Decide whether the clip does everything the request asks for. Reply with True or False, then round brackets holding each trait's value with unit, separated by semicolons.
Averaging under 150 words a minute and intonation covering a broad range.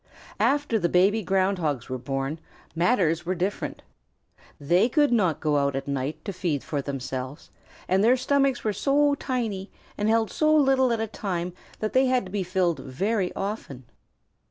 False (175 wpm; 7.1 semitones)